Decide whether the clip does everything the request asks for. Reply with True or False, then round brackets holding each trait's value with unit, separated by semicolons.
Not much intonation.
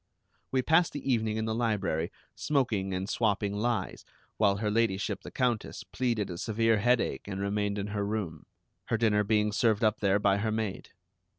True (2.2 semitones)